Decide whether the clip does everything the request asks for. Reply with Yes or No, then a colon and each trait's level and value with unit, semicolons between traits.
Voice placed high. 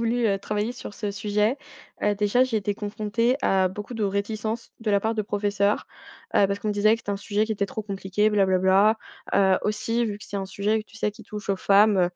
Yes: high, 210 Hz